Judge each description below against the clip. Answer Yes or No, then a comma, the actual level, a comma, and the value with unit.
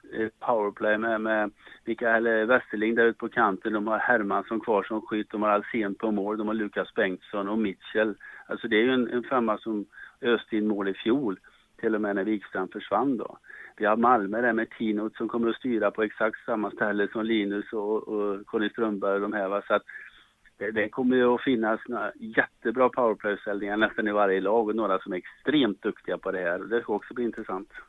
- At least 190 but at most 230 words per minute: Yes, fast, 205 wpm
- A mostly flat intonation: Yes, narrow, 1.7 semitones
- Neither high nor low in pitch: No, low, 110 Hz